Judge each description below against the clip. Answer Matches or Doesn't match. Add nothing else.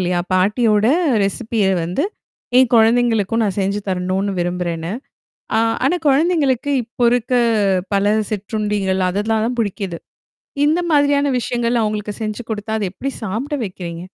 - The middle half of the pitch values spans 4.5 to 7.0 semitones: Doesn't match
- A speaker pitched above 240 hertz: Doesn't match